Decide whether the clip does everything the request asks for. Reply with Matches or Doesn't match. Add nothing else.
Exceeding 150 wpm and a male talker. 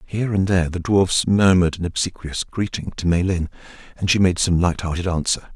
Matches